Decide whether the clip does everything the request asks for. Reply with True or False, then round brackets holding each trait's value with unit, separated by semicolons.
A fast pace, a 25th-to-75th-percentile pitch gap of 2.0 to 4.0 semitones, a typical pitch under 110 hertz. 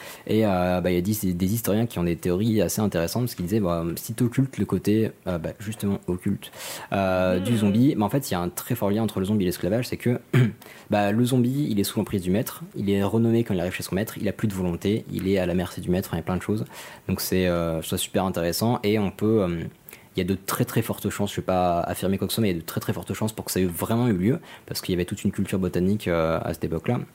True (305 wpm; 3.4 semitones; 100 Hz)